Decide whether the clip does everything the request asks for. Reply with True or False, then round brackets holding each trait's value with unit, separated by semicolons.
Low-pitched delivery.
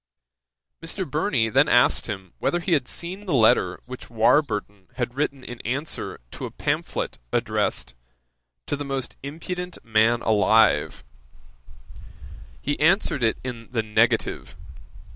True (130 Hz)